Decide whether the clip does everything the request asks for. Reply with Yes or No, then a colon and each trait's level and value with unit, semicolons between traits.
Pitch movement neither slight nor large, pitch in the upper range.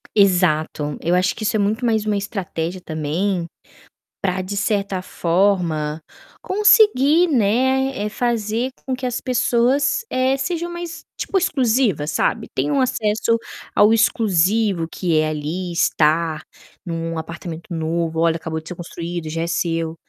No: wide, 6.4 semitones; high, 195 Hz